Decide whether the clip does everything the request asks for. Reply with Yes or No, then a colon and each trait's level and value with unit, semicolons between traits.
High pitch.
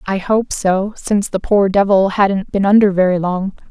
Yes: high, 195 Hz